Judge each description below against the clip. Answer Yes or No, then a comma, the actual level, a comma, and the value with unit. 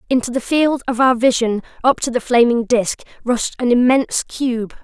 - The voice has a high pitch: Yes, high, 245 Hz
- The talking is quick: No, average, 185 wpm